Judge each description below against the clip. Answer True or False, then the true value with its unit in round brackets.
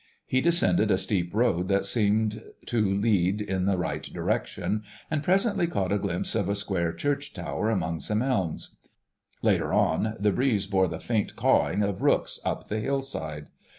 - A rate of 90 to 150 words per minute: False (170 wpm)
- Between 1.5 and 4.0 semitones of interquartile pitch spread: True (3.7 semitones)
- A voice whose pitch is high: False (105 Hz)